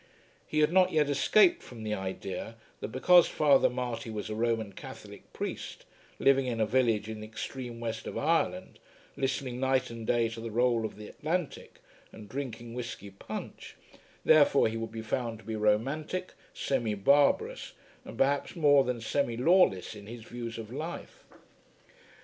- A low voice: Yes, low, 120 Hz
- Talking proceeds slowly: No, average, 165 wpm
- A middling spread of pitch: Yes, average, 3.9 semitones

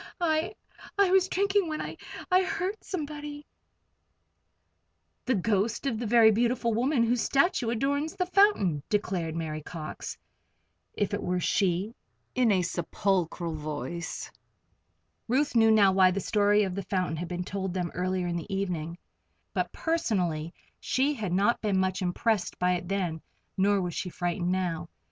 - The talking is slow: No, average, 160 wpm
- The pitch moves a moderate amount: No, wide, 6.1 semitones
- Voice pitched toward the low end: No, high, 200 Hz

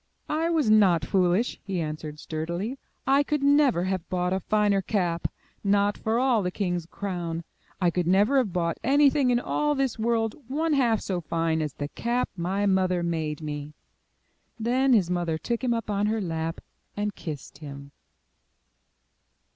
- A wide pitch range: Yes, wide, 5.9 semitones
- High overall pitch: Yes, high, 195 Hz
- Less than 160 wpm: No, average, 170 wpm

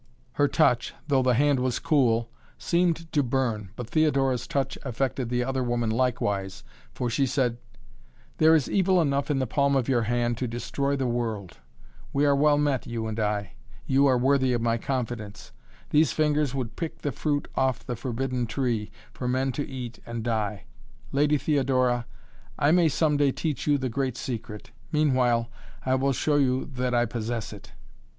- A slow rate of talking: No, average, 180 wpm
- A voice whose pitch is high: No, low, 130 Hz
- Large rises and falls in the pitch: No, average, 3.1 semitones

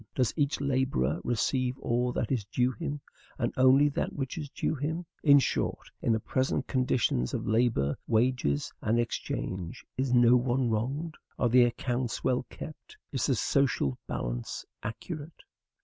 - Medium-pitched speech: No, low, 125 Hz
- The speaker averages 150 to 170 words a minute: Yes, average, 155 wpm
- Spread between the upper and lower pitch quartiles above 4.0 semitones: No, average, 3.1 semitones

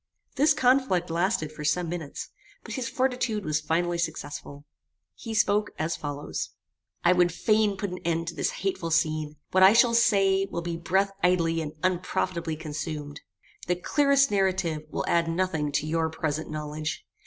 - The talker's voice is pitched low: No, medium, 170 Hz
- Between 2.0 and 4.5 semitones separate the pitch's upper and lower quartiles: Yes, average, 3.8 semitones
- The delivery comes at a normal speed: Yes, average, 165 wpm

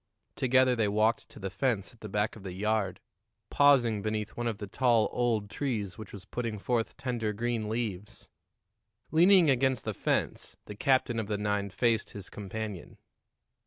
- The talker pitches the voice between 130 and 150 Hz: No, low, 110 Hz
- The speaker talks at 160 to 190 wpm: Yes, average, 170 wpm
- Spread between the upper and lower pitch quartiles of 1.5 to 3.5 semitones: Yes, average, 2.8 semitones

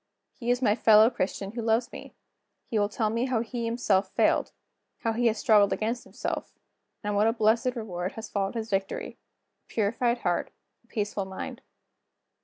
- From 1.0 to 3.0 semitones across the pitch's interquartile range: Yes, narrow, 2.5 semitones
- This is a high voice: Yes, high, 220 Hz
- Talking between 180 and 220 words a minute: Yes, average, 185 wpm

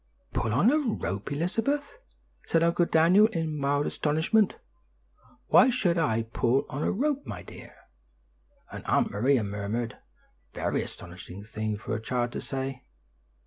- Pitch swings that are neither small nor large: No, wide, 9.0 semitones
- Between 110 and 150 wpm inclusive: Yes, average, 145 wpm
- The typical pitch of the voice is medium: Yes, medium, 145 Hz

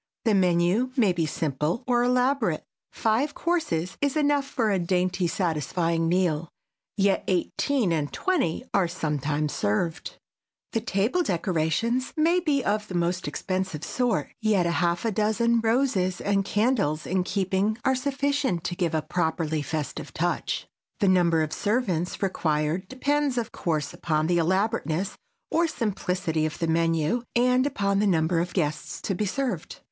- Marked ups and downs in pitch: Yes, wide, 6.3 semitones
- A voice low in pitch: No, medium, 185 Hz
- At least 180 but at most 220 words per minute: No, average, 150 wpm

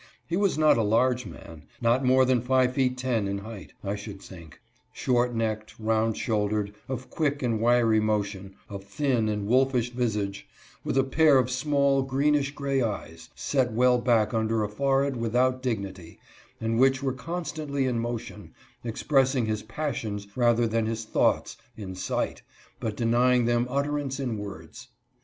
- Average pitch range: Yes, average, 3.5 semitones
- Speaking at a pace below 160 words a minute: No, average, 170 wpm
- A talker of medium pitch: No, low, 120 Hz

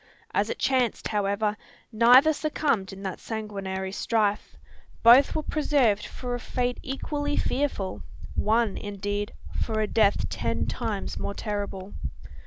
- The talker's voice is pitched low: No, high, 215 Hz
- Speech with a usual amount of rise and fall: Yes, average, 3.7 semitones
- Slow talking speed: Yes, slow, 130 wpm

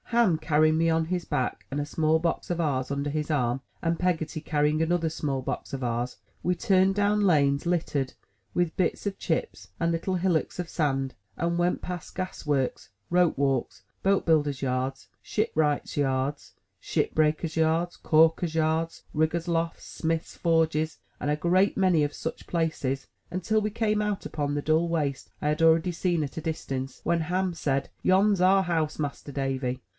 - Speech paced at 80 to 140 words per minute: No, average, 175 wpm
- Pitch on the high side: No, medium, 160 Hz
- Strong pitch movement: No, average, 3.3 semitones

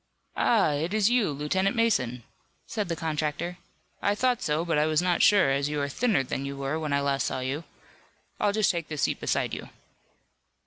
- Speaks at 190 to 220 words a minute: Yes, fast, 205 wpm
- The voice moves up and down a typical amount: No, wide, 5.8 semitones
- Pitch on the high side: No, medium, 155 Hz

